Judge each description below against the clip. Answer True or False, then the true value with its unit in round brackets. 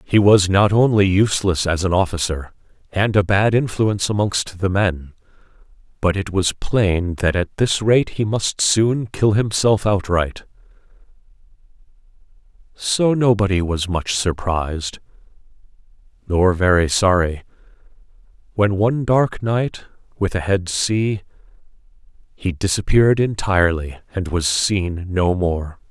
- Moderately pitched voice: False (95 Hz)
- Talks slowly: True (125 wpm)